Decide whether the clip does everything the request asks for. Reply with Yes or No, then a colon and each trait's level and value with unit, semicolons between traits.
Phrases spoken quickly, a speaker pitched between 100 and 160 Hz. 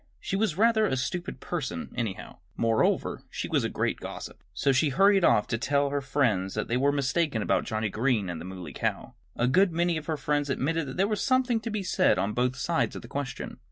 Yes: fast, 230 wpm; medium, 140 Hz